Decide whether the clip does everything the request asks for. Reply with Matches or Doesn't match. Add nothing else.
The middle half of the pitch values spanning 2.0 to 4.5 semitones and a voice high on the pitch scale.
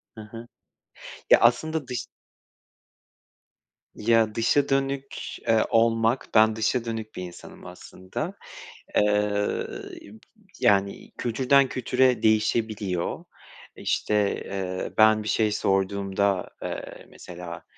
Doesn't match